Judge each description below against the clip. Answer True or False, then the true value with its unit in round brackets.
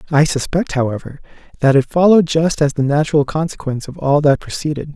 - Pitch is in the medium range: True (150 Hz)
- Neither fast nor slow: True (180 wpm)